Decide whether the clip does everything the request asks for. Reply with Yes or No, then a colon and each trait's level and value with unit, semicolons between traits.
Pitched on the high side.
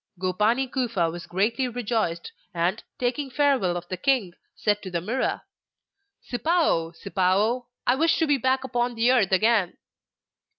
Yes: high, 230 Hz